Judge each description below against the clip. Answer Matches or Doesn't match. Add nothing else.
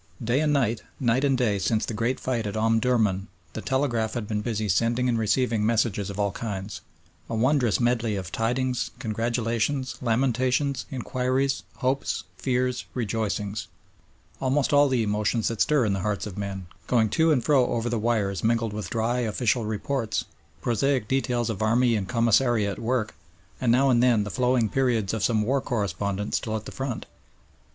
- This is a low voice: Matches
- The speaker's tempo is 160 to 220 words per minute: Matches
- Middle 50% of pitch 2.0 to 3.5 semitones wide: Matches